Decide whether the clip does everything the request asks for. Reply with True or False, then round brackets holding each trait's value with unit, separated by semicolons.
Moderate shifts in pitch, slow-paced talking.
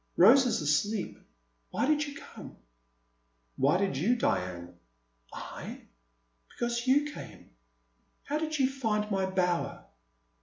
False (7.2 semitones; 120 wpm)